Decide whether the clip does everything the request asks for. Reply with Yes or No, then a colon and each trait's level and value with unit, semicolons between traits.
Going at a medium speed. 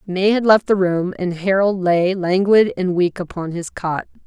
Yes: average, 195 wpm